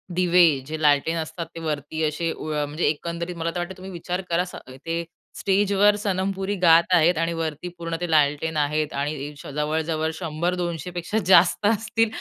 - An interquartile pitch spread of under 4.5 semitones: Yes, narrow, 2.6 semitones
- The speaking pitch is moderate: Yes, medium, 170 Hz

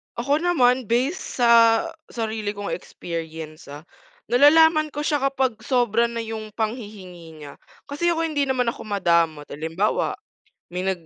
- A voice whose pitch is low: No, high, 225 Hz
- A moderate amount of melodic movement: No, wide, 7.3 semitones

